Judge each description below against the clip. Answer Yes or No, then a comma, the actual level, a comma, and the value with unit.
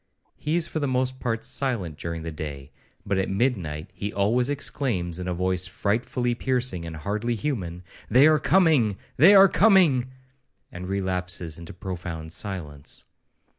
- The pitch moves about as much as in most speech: No, wide, 6.9 semitones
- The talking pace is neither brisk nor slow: Yes, average, 155 wpm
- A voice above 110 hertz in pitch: No, low, 100 Hz